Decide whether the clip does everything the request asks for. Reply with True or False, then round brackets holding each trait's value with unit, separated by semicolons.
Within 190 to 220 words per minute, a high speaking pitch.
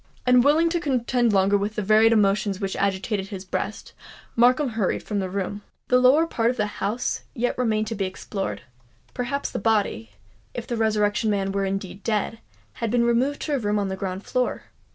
False (180 wpm; 210 Hz)